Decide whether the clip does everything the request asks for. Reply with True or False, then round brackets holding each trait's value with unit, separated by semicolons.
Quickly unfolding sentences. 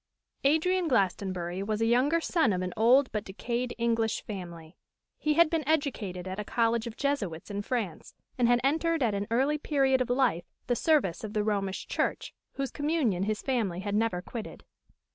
False (185 wpm)